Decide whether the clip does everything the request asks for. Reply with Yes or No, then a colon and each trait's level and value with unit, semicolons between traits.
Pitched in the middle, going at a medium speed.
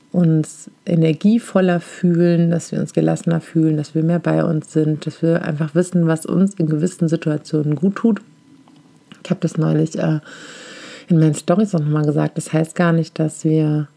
Yes: medium, 165 Hz; average, 175 wpm